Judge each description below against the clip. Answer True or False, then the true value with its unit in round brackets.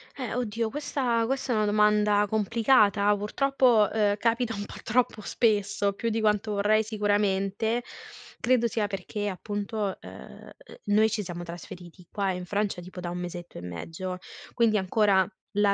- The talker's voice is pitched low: False (210 Hz)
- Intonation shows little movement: True (2.3 semitones)